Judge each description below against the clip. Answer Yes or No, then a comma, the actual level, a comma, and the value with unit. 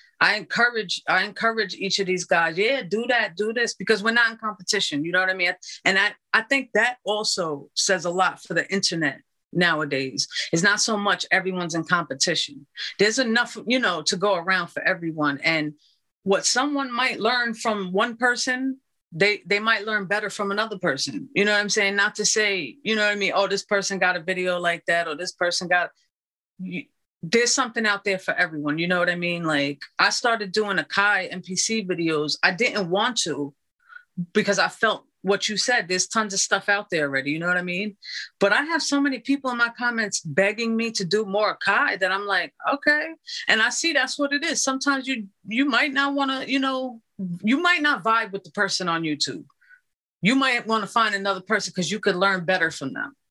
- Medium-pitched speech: No, high, 205 Hz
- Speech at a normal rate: No, fast, 215 wpm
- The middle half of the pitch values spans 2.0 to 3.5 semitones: No, average, 4.7 semitones